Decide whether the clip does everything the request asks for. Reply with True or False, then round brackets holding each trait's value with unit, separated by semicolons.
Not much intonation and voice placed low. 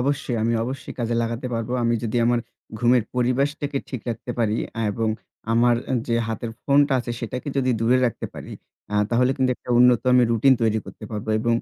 True (1.8 semitones; 120 Hz)